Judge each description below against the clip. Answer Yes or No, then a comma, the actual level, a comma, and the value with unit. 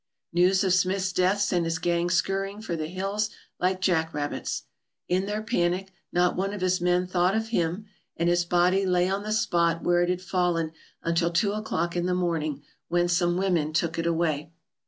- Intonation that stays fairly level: Yes, narrow, 2.0 semitones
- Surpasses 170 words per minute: Yes, average, 195 wpm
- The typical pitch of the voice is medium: Yes, medium, 180 Hz